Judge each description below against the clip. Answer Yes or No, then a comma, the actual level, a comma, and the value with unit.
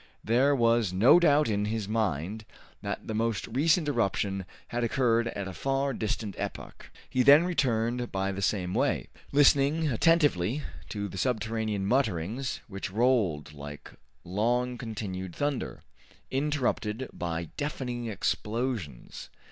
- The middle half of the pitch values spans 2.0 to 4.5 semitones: No, average, 5.1 semitones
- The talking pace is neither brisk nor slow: No, slow, 130 wpm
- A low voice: Yes, low, 115 Hz